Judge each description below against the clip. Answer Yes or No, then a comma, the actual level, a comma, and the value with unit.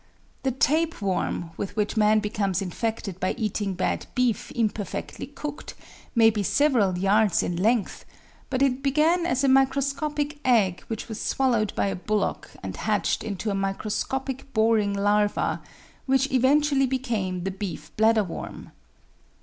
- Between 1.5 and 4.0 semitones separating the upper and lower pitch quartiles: No, average, 4.9 semitones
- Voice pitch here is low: No, high, 220 Hz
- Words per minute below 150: Yes, average, 140 wpm